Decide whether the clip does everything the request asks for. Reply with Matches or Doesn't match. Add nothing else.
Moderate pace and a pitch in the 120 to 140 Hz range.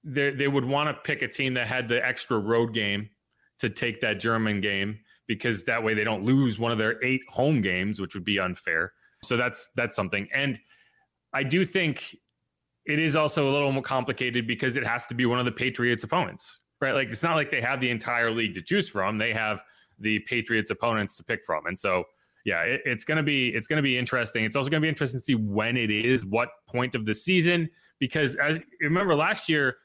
Doesn't match